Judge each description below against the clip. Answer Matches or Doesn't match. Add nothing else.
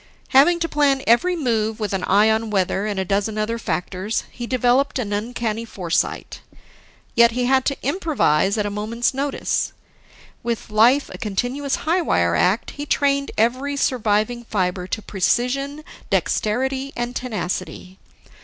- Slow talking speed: Doesn't match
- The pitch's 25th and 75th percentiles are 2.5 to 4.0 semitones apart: Doesn't match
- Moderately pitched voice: Doesn't match